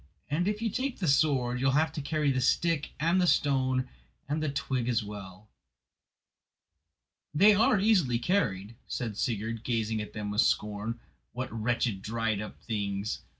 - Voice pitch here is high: No, low, 125 Hz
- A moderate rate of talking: Yes, average, 165 wpm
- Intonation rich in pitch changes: Yes, wide, 6.2 semitones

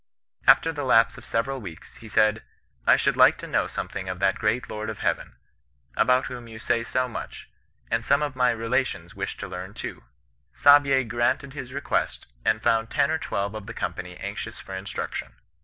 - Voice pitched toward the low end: Yes, low, 115 Hz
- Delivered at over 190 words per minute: Yes, average, 200 wpm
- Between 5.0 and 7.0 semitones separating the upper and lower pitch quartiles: No, average, 4.0 semitones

